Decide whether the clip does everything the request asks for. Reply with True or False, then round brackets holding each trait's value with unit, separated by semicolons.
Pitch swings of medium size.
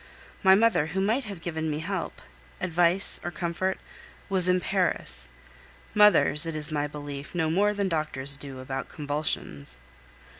True (4.5 semitones)